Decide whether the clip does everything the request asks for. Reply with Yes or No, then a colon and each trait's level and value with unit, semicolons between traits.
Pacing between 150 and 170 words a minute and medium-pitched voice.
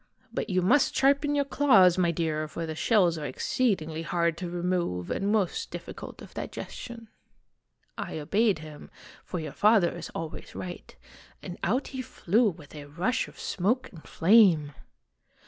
Yes: average, 165 wpm; medium, 180 Hz